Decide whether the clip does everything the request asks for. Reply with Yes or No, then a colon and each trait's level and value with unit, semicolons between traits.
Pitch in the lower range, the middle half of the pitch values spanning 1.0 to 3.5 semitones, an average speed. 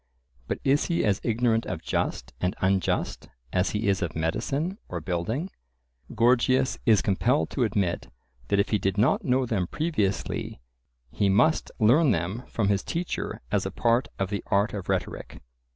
No: low, 105 Hz; average, 5.0 semitones; average, 170 wpm